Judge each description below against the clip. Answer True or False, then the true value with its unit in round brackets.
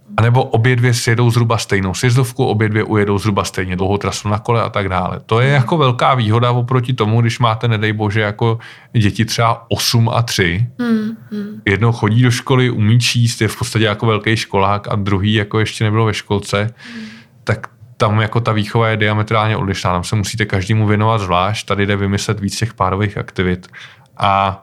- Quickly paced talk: True (190 wpm)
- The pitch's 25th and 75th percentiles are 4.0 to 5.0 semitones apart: False (2.7 semitones)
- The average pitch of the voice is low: True (110 Hz)